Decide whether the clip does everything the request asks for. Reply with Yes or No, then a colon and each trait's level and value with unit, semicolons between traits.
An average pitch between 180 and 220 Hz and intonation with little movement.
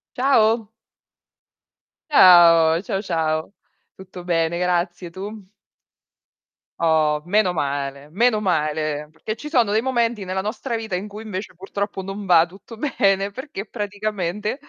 No: high, 190 Hz; average, 4.2 semitones